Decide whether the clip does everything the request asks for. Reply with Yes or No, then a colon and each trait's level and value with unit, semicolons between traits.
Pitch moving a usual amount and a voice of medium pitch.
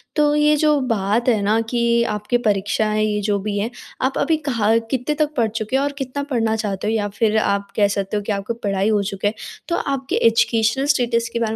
No: average, 3.8 semitones; high, 225 Hz